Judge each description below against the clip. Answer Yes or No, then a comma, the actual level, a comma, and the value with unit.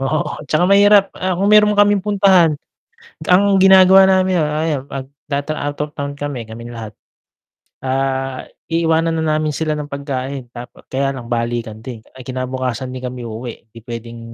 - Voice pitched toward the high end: No, medium, 140 Hz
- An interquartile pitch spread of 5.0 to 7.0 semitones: Yes, average, 5.3 semitones